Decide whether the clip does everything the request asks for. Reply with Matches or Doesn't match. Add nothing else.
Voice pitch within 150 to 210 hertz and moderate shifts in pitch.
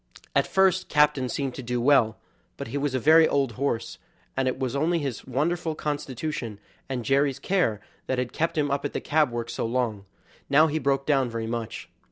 Doesn't match